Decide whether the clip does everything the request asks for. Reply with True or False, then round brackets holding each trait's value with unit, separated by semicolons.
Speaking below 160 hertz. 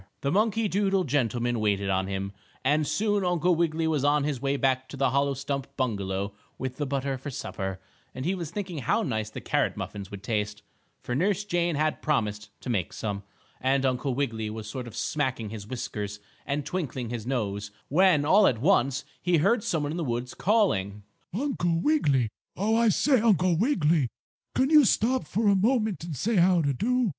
True (140 Hz)